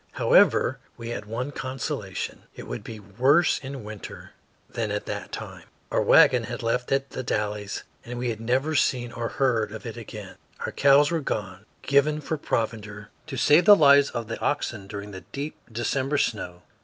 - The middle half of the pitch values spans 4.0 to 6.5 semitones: Yes, average, 4.6 semitones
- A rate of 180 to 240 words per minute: Yes, average, 185 wpm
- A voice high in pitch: No, low, 120 Hz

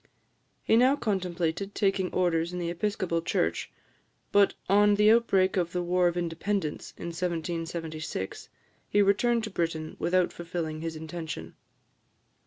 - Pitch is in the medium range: Yes, medium, 175 Hz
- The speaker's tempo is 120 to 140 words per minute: Yes, slow, 135 wpm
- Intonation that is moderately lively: Yes, average, 3.3 semitones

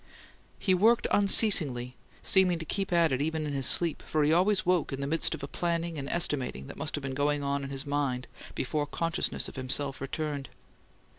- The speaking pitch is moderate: Yes, medium, 150 Hz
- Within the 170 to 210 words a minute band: Yes, fast, 205 wpm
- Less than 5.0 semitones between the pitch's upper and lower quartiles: Yes, average, 3.7 semitones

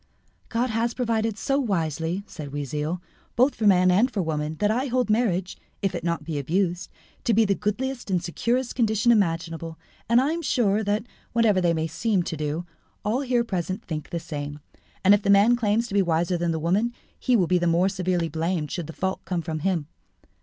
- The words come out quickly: Yes, fast, 210 wpm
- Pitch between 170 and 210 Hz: Yes, high, 190 Hz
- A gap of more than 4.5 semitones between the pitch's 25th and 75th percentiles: Yes, wide, 5.4 semitones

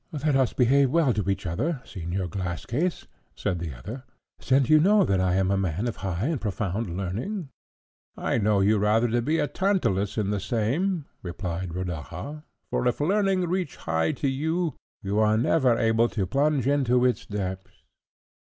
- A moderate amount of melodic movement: No, wide, 7.2 semitones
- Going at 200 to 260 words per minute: No, average, 175 wpm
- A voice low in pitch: Yes, low, 115 Hz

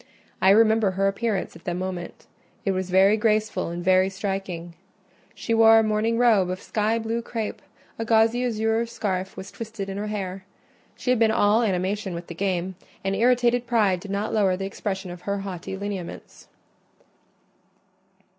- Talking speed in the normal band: Yes, average, 165 wpm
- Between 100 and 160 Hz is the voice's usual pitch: No, high, 200 Hz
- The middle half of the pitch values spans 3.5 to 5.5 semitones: No, average, 2.9 semitones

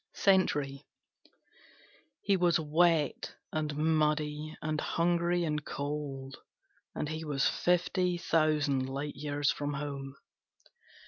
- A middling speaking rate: No, slow, 105 wpm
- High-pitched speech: No, medium, 150 Hz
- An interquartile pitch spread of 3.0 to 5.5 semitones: No, narrow, 2.5 semitones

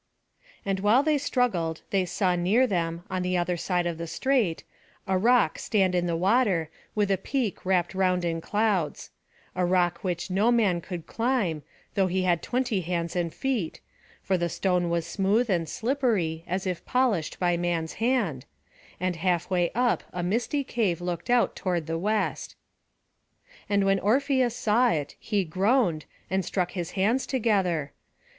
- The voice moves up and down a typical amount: Yes, average, 4.4 semitones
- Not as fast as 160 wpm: No, average, 165 wpm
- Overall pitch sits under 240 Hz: Yes, medium, 185 Hz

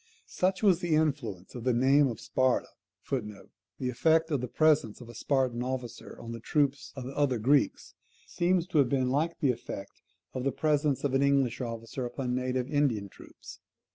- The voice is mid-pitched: No, low, 130 Hz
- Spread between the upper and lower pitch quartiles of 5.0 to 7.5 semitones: No, average, 3.4 semitones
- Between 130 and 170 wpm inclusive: No, average, 185 wpm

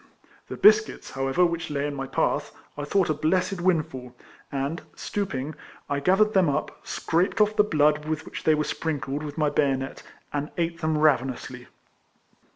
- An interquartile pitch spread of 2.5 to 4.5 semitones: Yes, average, 3.7 semitones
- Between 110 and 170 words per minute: Yes, average, 165 wpm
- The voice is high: No, medium, 155 Hz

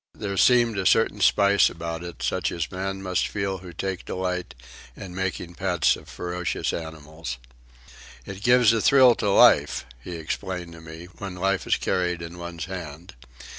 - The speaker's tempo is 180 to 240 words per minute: No, average, 170 wpm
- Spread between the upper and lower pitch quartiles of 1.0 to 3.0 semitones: Yes, narrow, 2.4 semitones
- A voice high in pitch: No, very low, 90 Hz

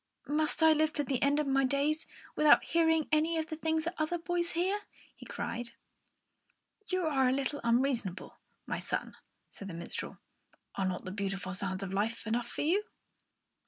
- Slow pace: No, average, 180 wpm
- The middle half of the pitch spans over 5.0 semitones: Yes, wide, 5.6 semitones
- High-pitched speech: Yes, very high, 285 Hz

